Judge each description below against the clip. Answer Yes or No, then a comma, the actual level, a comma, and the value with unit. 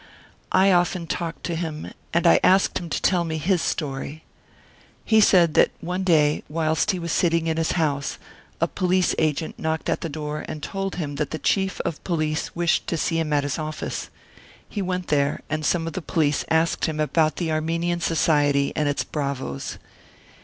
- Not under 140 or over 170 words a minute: No, average, 190 wpm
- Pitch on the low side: No, medium, 160 Hz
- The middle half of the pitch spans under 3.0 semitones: Yes, narrow, 2.4 semitones